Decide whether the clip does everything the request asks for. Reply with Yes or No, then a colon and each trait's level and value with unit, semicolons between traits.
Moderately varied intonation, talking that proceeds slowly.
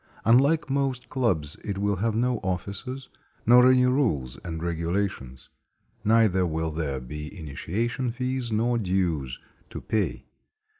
No: wide, 7.3 semitones; slow, 130 wpm